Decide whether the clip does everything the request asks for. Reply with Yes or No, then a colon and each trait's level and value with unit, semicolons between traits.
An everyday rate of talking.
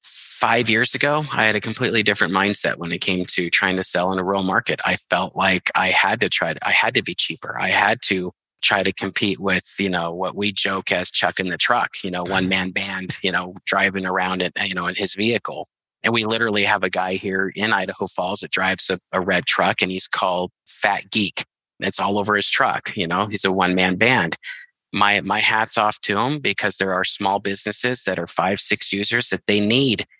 No: fast, 230 wpm